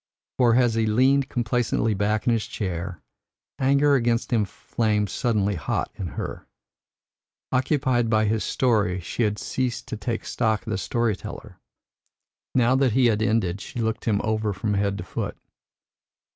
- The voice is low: Yes, low, 110 Hz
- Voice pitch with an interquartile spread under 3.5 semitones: Yes, average, 2.9 semitones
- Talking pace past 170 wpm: No, average, 160 wpm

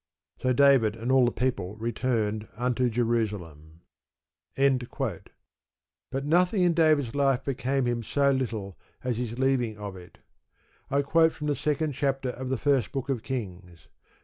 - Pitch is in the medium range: No, low, 125 Hz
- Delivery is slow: No, average, 150 wpm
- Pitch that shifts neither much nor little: Yes, average, 3.8 semitones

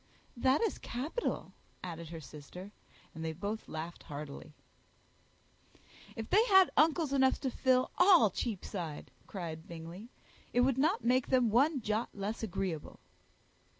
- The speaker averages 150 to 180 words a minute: No, slow, 135 wpm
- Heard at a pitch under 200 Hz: No, high, 220 Hz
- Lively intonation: Yes, wide, 7.8 semitones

